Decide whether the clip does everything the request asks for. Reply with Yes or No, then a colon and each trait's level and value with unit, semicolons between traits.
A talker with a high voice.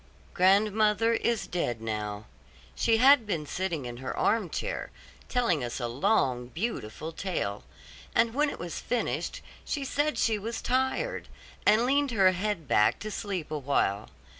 Yes: high, 195 Hz